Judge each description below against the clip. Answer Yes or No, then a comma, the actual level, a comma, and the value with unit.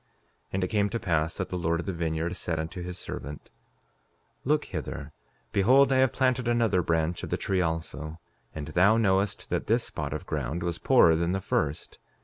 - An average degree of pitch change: Yes, average, 4.0 semitones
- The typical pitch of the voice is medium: No, very low, 90 Hz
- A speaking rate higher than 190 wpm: Yes, average, 200 wpm